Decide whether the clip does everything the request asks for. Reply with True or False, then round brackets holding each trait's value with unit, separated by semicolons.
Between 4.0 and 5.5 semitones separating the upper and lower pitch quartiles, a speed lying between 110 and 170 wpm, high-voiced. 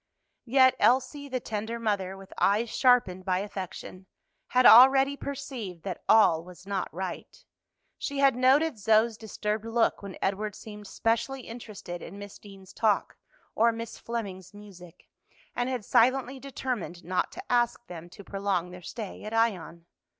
True (4.4 semitones; 150 wpm; 215 Hz)